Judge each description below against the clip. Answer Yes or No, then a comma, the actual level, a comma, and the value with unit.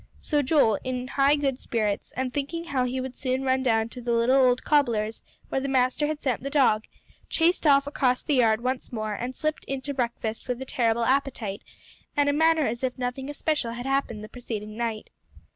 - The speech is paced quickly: Yes, fast, 210 wpm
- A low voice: No, very high, 255 Hz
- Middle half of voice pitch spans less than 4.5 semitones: Yes, average, 3.1 semitones